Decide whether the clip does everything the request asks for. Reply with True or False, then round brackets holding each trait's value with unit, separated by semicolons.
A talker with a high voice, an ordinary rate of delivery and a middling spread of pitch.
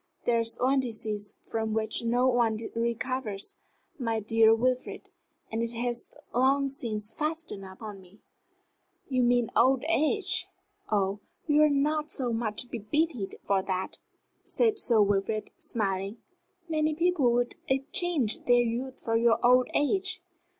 True (240 Hz; 145 wpm; 4.0 semitones)